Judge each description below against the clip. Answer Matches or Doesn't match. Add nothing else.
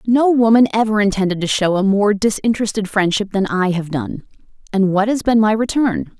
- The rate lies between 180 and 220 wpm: Matches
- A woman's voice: Matches